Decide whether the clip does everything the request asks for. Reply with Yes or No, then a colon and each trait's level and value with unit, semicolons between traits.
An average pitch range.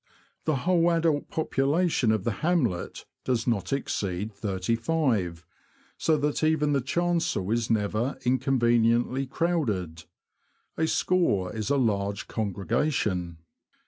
No: wide, 7.1 semitones